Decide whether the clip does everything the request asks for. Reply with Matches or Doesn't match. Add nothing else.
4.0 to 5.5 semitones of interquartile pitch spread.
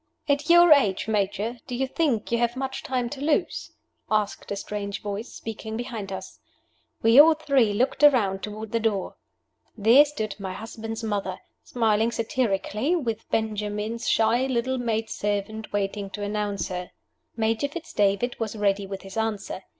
Doesn't match